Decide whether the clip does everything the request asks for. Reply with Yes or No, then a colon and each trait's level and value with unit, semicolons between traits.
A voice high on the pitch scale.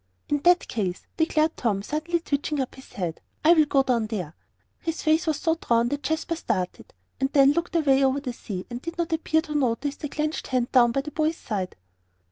Yes: very high, 280 Hz